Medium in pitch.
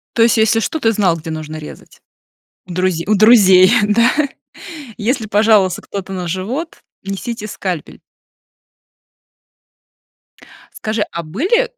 No: high, 205 Hz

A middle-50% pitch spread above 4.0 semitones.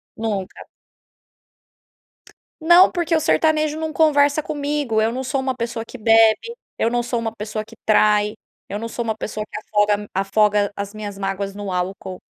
Yes: average, 5.0 semitones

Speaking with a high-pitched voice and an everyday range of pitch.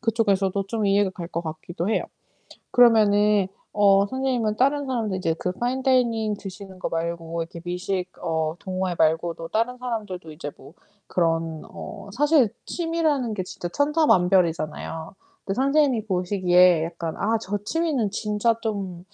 Yes: high, 200 Hz; average, 5.0 semitones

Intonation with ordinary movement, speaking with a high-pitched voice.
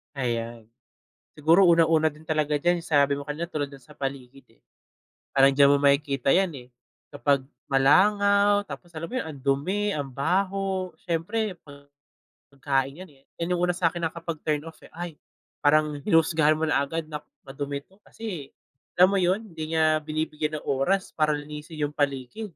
No: average, 3.8 semitones; medium, 155 Hz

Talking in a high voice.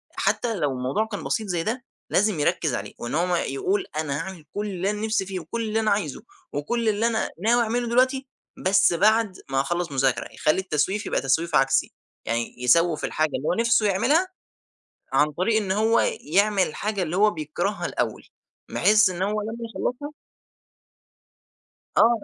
Yes: high, 195 Hz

